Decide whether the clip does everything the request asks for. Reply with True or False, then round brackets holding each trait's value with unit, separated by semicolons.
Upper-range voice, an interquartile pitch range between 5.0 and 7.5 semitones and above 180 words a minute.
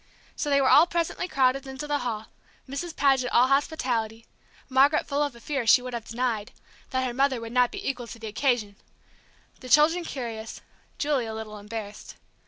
False (255 Hz; 3.6 semitones; 190 wpm)